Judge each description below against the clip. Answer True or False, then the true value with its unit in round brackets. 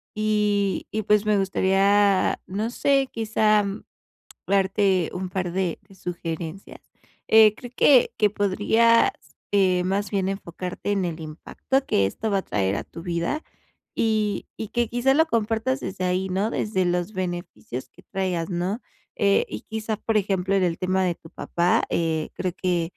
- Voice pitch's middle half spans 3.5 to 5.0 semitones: False (3.1 semitones)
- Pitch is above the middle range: True (195 Hz)